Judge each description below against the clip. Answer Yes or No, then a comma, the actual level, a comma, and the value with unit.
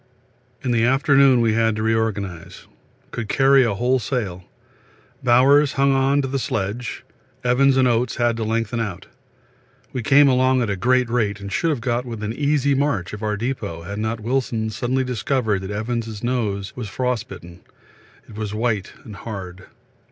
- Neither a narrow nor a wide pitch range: Yes, average, 3.5 semitones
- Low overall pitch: Yes, low, 115 Hz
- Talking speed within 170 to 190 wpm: Yes, average, 175 wpm